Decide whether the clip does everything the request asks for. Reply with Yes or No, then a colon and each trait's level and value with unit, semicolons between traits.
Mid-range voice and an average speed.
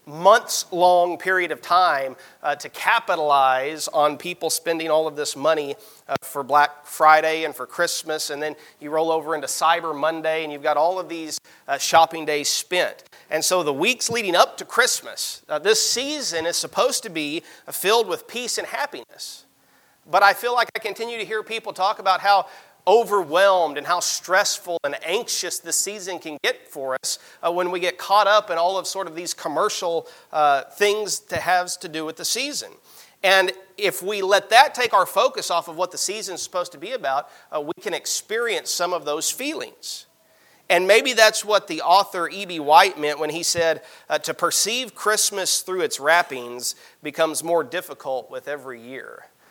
Yes: medium, 175 Hz; average, 190 wpm